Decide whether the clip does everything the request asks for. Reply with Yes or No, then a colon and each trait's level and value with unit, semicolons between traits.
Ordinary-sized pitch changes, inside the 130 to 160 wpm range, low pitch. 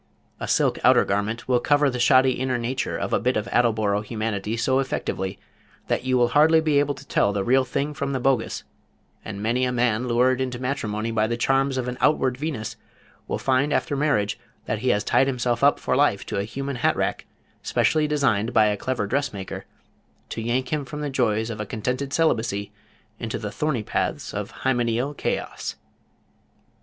No: average, 3.6 semitones; average, 190 wpm; low, 125 Hz